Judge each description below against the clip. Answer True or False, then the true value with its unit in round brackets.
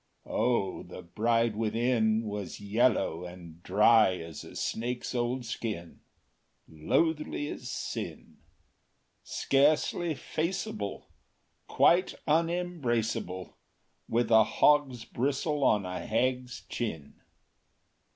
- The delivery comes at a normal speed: False (95 wpm)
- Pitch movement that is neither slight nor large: True (4.7 semitones)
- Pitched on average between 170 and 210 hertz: False (115 Hz)